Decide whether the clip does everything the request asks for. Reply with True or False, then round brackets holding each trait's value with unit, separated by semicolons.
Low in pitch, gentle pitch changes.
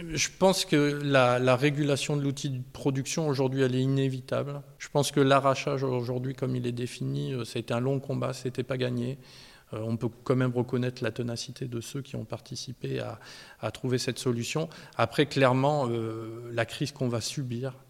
True (130 Hz; 2.2 semitones)